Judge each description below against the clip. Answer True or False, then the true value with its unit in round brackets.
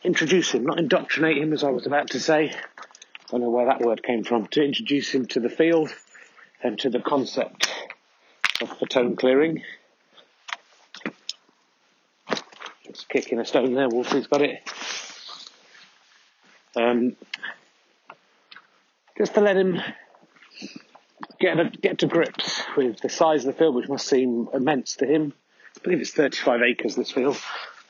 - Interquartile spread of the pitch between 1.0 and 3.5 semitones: False (4.5 semitones)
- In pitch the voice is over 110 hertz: True (140 Hz)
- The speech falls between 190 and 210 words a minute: False (150 wpm)